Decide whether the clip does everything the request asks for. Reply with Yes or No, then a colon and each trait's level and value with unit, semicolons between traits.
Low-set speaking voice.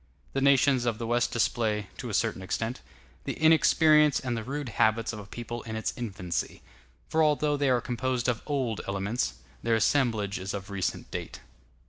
Yes: low, 120 Hz